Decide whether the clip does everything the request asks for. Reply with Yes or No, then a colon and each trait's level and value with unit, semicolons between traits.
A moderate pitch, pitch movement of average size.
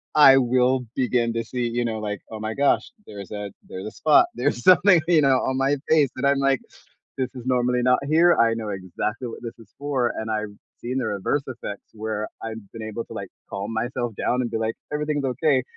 No: low, 120 Hz; average, 3.5 semitones